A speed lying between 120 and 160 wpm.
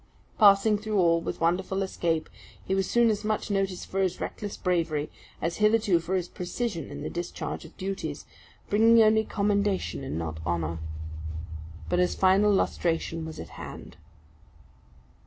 Yes: average, 155 wpm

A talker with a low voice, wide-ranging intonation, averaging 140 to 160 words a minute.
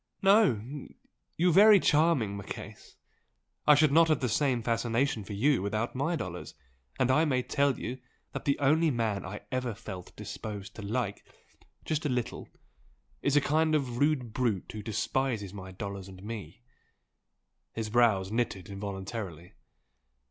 Yes: low, 120 Hz; wide, 5.8 semitones; average, 150 wpm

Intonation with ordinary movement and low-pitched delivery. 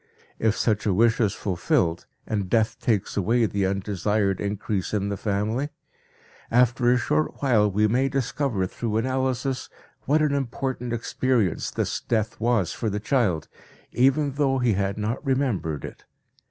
Yes: average, 4.1 semitones; low, 115 Hz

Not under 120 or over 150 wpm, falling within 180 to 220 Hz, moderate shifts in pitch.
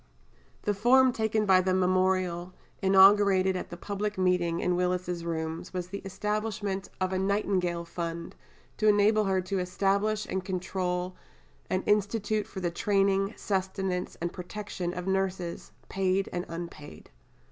No: average, 140 wpm; high, 190 Hz; narrow, 2.0 semitones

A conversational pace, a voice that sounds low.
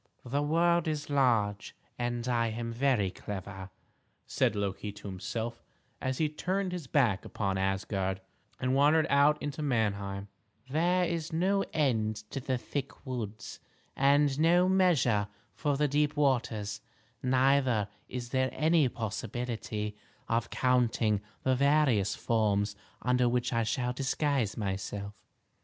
No: slow, 130 wpm; low, 125 Hz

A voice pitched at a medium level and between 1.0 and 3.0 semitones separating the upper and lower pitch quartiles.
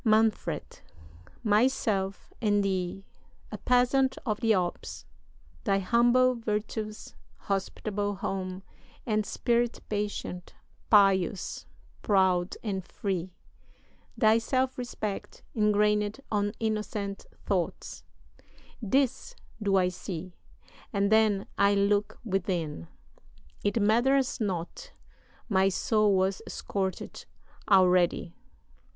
No: high, 205 Hz; narrow, 2.5 semitones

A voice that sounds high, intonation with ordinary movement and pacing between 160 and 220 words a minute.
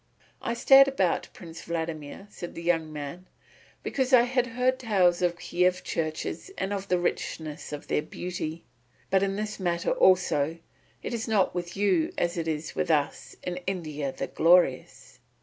No: medium, 175 Hz; average, 3.5 semitones; average, 165 wpm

